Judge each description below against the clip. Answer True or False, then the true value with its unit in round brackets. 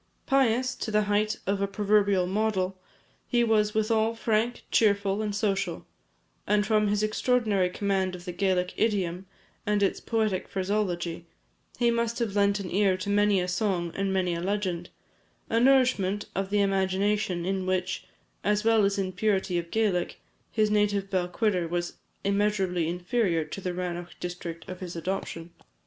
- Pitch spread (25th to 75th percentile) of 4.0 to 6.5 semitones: False (2.7 semitones)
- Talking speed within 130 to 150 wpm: False (160 wpm)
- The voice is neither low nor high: False (200 Hz)